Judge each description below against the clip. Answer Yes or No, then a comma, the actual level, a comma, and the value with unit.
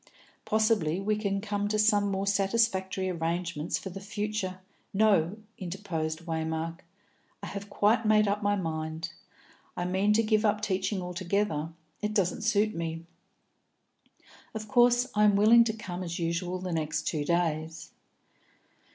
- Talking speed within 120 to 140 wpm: No, average, 150 wpm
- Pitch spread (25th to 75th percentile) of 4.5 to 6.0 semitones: No, average, 3.9 semitones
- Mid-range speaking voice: No, high, 195 Hz